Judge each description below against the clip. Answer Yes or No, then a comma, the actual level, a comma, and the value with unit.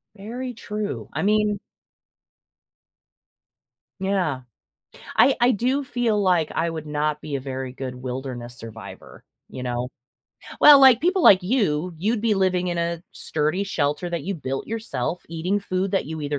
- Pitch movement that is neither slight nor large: No, wide, 6.3 semitones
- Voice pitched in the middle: Yes, medium, 180 Hz